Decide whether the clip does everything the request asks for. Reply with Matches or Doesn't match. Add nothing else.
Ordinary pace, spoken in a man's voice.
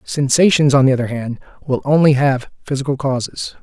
Matches